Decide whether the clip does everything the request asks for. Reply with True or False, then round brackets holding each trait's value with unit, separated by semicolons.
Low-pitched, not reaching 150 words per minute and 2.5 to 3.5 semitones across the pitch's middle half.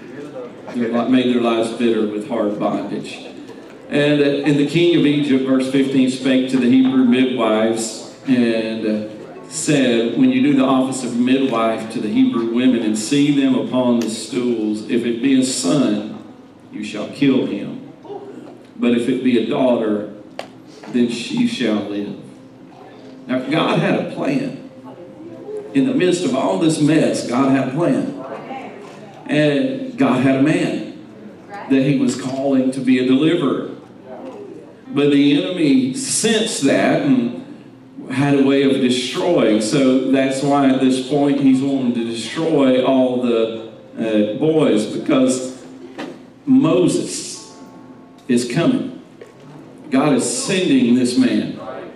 False (130 Hz; 140 wpm; 4.0 semitones)